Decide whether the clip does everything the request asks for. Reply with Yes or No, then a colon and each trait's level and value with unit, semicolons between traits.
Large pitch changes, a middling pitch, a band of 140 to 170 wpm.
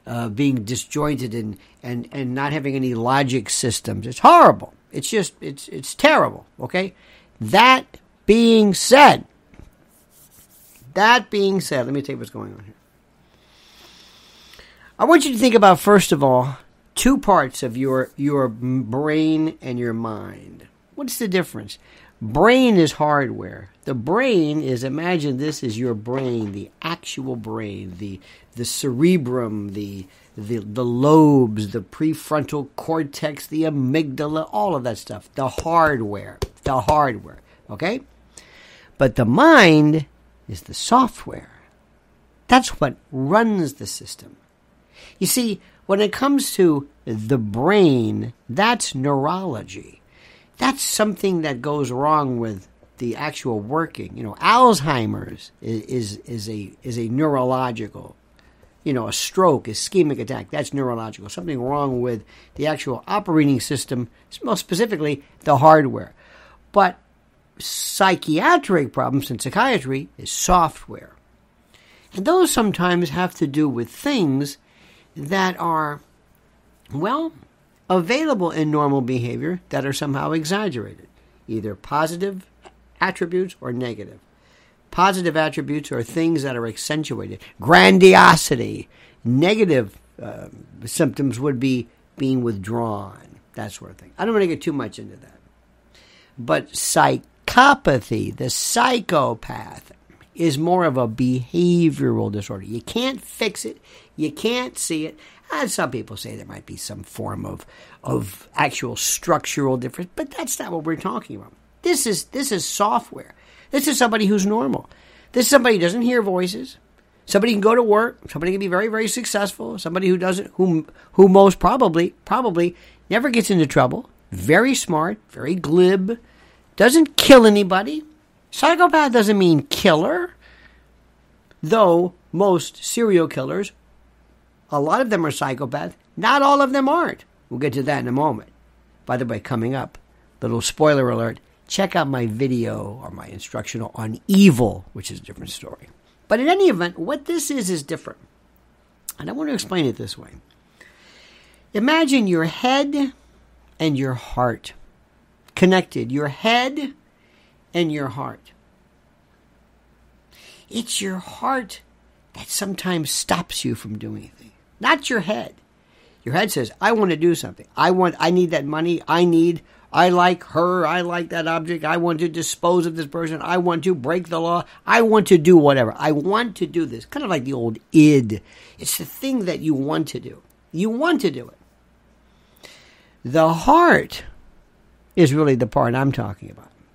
Yes: wide, 7.5 semitones; medium, 155 Hz; average, 145 wpm